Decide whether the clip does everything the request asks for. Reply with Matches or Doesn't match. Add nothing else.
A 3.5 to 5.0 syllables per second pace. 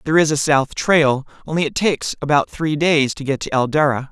Doesn't match